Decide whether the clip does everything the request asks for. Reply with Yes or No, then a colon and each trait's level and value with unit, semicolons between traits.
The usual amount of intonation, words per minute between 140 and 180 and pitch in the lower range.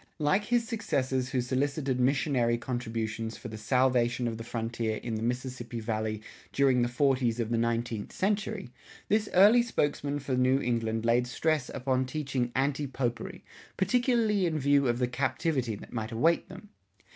Yes: average, 3.6 semitones; average, 160 wpm; low, 130 Hz